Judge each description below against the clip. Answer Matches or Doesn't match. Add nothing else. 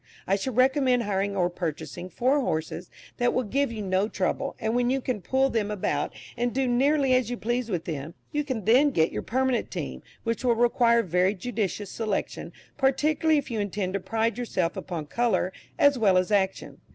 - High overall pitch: Matches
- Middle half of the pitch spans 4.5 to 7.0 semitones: Matches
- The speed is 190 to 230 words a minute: Matches